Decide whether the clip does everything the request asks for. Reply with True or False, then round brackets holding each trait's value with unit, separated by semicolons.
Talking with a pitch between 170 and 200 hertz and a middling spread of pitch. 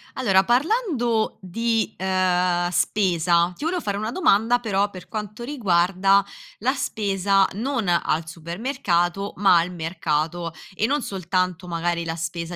True (190 Hz; 4.3 semitones)